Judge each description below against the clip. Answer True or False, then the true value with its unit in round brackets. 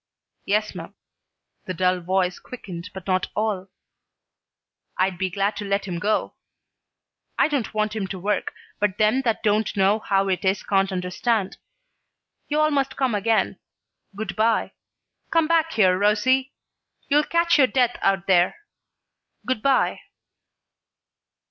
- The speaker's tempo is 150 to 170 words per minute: False (140 wpm)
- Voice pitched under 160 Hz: False (210 Hz)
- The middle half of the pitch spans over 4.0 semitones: True (4.4 semitones)